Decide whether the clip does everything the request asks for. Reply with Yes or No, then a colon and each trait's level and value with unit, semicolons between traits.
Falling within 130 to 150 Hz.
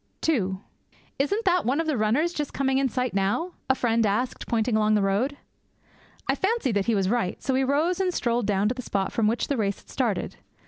No: high, 245 Hz